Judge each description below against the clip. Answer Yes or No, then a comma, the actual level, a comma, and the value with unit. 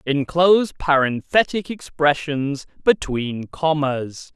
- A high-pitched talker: No, medium, 150 Hz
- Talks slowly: Yes, slow, 70 wpm